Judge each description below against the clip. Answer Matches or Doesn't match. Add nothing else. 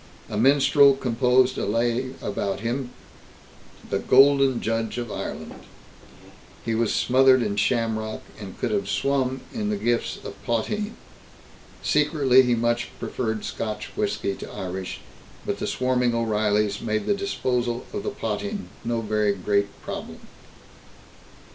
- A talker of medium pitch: Doesn't match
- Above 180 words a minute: Doesn't match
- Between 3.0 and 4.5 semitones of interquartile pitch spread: Matches